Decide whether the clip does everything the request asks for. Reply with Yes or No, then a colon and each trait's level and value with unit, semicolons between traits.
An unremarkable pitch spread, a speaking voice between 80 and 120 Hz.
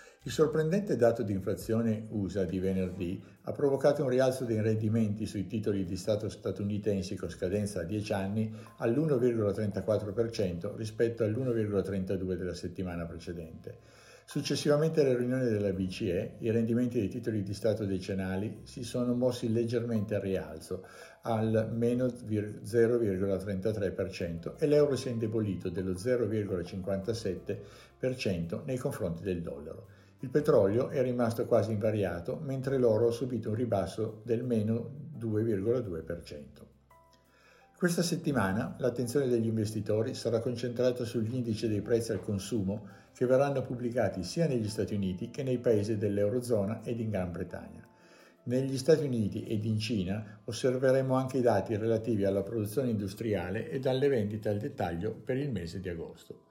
Yes: average, 3.8 semitones; low, 110 Hz